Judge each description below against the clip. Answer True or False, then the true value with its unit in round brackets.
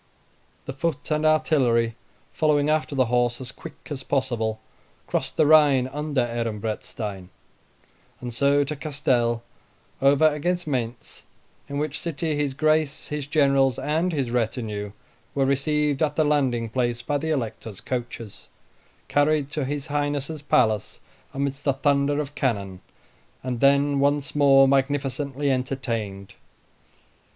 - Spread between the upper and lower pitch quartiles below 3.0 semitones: False (3.3 semitones)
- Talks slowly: True (130 wpm)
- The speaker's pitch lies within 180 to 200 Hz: False (140 Hz)